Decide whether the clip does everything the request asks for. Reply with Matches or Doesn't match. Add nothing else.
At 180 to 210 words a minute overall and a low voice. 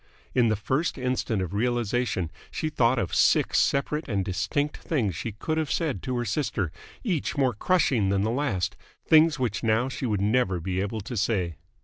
Matches